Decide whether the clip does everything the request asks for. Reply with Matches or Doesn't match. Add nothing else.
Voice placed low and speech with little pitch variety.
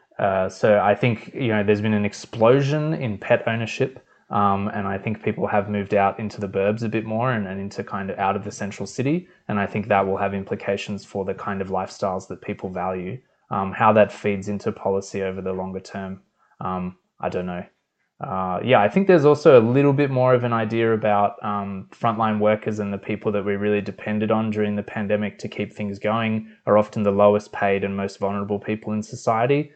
Matches